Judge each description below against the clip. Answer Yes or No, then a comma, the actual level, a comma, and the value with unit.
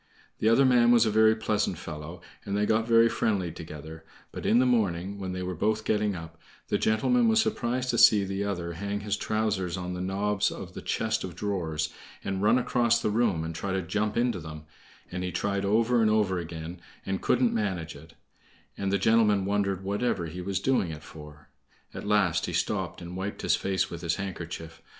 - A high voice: No, low, 100 Hz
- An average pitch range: Yes, average, 3.9 semitones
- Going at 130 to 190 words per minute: No, fast, 205 wpm